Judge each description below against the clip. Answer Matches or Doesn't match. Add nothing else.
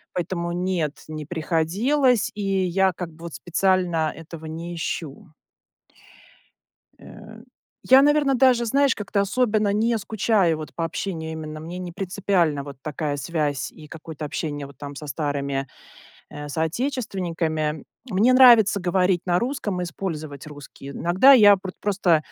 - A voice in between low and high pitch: Matches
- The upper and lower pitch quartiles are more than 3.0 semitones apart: Matches